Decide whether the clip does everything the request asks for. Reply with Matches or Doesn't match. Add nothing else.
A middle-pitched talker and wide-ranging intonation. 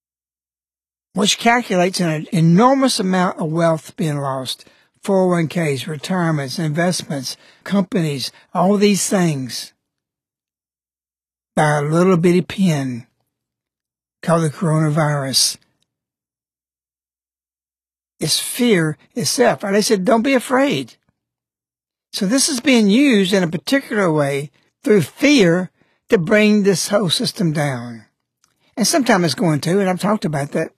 Matches